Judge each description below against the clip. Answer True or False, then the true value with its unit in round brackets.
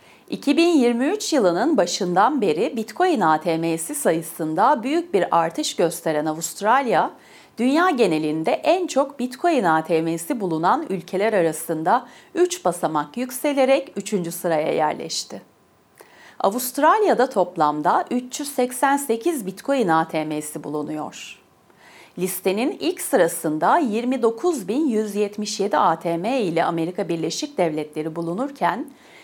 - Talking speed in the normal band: False (90 wpm)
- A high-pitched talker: True (205 Hz)